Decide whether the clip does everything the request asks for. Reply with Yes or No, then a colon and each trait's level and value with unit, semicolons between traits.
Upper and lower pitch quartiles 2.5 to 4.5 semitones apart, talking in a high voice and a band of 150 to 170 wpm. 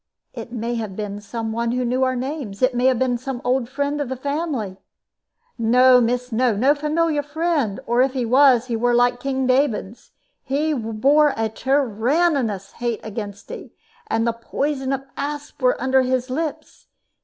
No: average, 3.2 semitones; very high, 255 Hz; average, 180 wpm